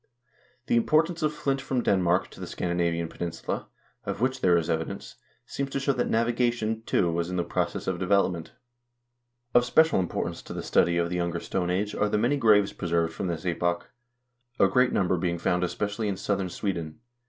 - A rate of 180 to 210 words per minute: Yes, average, 190 wpm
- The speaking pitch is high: No, very low, 95 Hz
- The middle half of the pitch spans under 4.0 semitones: No, wide, 5.5 semitones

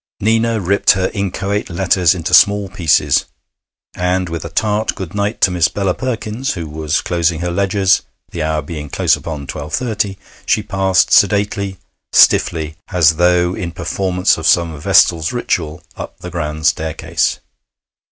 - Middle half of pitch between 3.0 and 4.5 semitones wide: Yes, average, 3.7 semitones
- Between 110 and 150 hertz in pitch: No, very low, 90 Hz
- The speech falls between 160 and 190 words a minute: No, average, 150 wpm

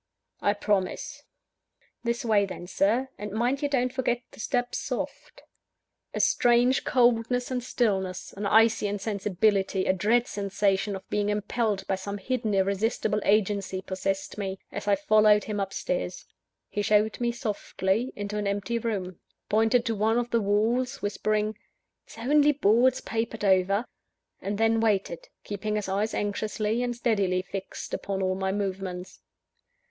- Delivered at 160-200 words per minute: No, average, 150 wpm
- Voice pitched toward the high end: Yes, high, 210 Hz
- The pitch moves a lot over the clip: No, average, 3.0 semitones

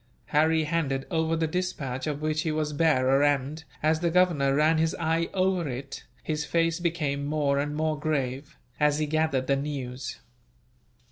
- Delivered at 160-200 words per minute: Yes, average, 165 wpm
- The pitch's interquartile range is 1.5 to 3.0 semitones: Yes, narrow, 2.5 semitones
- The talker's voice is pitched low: No, medium, 155 Hz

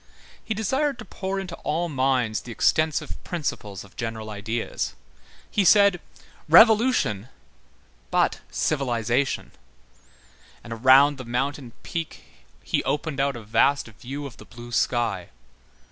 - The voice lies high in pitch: No, low, 135 Hz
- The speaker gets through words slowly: Yes, slow, 125 wpm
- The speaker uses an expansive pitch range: Yes, wide, 6.3 semitones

